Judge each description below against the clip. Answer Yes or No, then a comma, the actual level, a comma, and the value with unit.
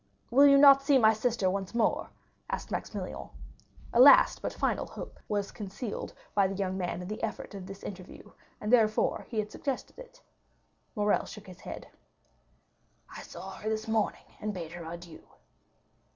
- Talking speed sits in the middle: Yes, average, 170 wpm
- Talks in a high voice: Yes, high, 210 Hz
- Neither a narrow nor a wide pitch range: Yes, average, 3.9 semitones